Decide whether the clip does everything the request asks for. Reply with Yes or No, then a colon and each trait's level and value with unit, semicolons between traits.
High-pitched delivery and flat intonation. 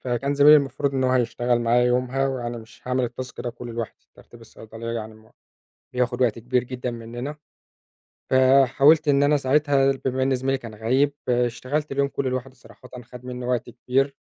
No: low, 125 Hz; narrow, 2.1 semitones